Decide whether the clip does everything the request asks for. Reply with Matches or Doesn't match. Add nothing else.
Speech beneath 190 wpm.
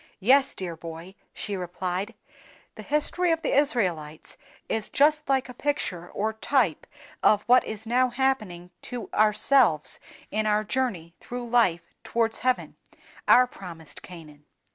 Matches